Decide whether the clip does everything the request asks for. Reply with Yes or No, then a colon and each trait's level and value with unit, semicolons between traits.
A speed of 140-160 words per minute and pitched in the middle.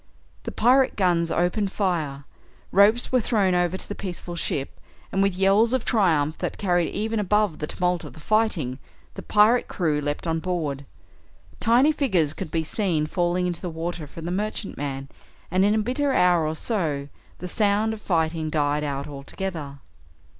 No: average, 175 wpm; medium, 180 Hz